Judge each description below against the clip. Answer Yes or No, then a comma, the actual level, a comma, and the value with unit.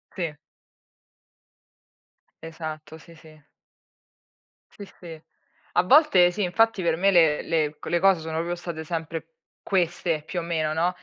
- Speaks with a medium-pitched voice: Yes, medium, 165 Hz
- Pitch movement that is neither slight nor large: No, narrow, 2.0 semitones